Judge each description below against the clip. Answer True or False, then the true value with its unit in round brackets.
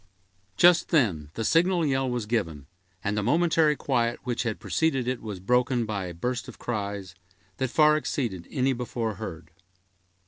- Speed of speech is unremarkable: True (165 wpm)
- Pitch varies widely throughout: False (4.8 semitones)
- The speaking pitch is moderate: False (120 Hz)